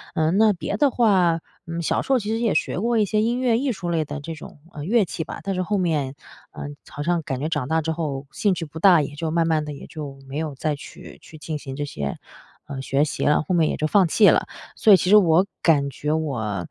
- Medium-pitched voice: Yes, medium, 160 Hz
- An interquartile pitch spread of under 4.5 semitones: No, average, 5.0 semitones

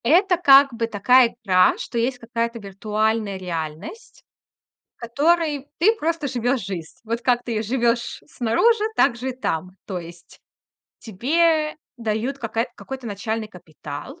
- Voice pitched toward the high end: Yes, high, 235 Hz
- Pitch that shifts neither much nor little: Yes, average, 4.7 semitones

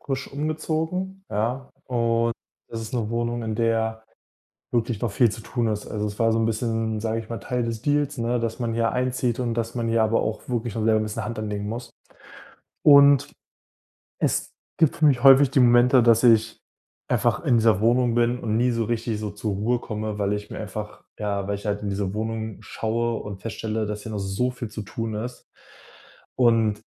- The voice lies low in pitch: Yes, low, 115 Hz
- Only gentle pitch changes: Yes, narrow, 2.1 semitones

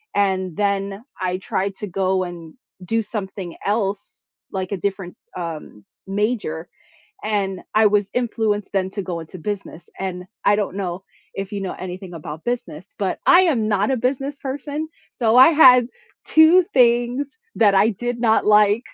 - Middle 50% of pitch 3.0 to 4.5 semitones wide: Yes, average, 4.0 semitones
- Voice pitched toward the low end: No, high, 200 Hz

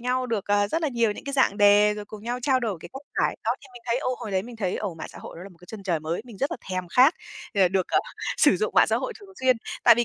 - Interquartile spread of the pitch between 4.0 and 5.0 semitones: Yes, average, 4.6 semitones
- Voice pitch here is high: Yes, high, 215 Hz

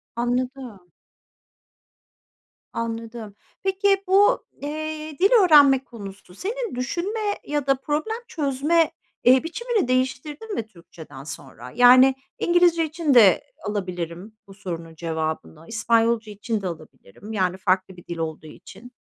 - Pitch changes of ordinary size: No, wide, 8.4 semitones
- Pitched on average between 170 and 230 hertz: No, high, 245 Hz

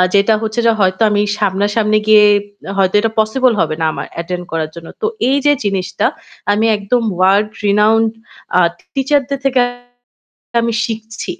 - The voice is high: Yes, high, 210 Hz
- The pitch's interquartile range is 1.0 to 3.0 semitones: Yes, average, 2.7 semitones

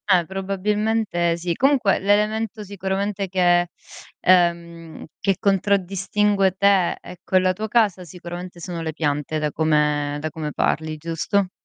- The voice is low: No, medium, 185 Hz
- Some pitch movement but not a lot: Yes, average, 3.2 semitones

